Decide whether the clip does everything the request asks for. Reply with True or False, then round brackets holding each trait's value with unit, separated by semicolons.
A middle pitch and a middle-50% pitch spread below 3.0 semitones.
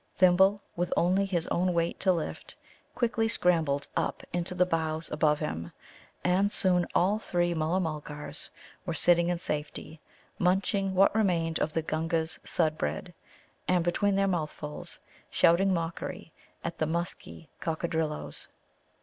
True (170 Hz; 2.6 semitones)